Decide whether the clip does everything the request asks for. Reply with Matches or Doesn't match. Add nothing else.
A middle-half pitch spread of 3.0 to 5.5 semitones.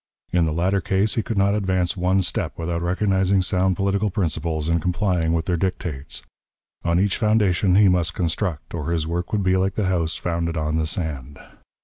Doesn't match